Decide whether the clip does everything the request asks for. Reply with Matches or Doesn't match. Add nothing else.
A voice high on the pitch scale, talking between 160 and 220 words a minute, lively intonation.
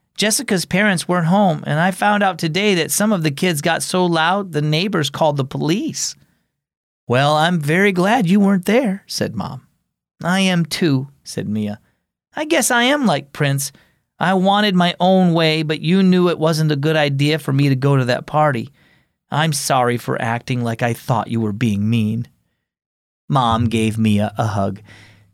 Doesn't match